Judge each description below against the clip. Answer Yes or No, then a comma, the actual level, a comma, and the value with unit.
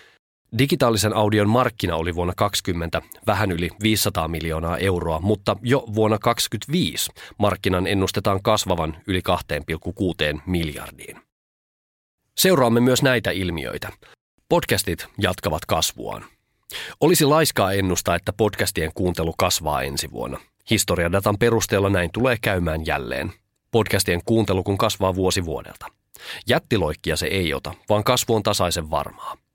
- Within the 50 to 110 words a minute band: No, average, 120 wpm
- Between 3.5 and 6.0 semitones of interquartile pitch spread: Yes, average, 3.9 semitones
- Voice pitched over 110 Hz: No, low, 100 Hz